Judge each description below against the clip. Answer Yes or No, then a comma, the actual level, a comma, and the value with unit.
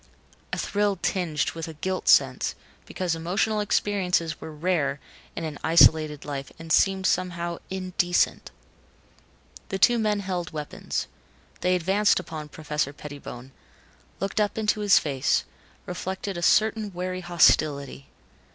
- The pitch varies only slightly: No, average, 3.8 semitones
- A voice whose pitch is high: No, medium, 175 Hz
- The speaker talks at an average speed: No, slow, 130 wpm